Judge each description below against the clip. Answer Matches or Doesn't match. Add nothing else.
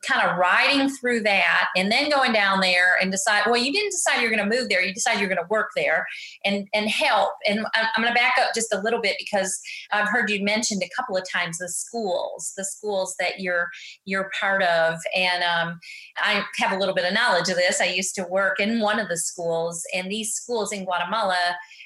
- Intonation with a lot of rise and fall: Doesn't match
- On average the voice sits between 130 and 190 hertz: Doesn't match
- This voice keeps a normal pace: Doesn't match